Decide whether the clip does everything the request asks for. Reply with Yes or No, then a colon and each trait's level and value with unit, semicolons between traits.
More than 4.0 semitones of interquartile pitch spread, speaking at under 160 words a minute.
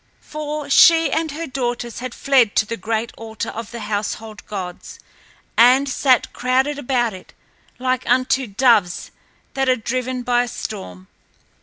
No: average, 3.2 semitones; average, 150 wpm